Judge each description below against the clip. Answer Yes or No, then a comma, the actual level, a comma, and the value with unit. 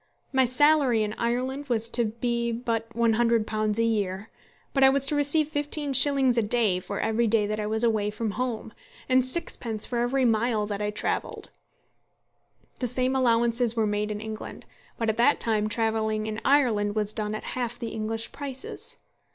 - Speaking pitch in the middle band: No, high, 230 Hz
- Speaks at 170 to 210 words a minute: Yes, average, 180 wpm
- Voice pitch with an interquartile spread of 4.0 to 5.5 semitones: No, average, 2.9 semitones